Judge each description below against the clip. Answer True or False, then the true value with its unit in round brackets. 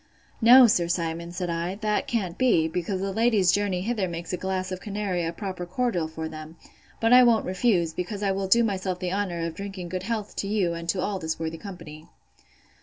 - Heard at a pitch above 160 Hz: True (185 Hz)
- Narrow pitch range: False (3.3 semitones)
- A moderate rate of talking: False (215 wpm)